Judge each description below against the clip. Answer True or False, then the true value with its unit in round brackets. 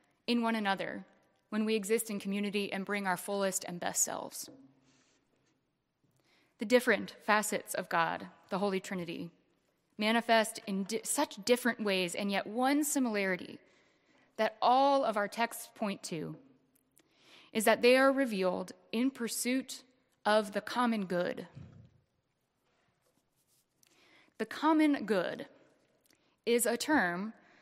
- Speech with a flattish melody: False (4.3 semitones)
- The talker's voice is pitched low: False (220 Hz)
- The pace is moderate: False (125 wpm)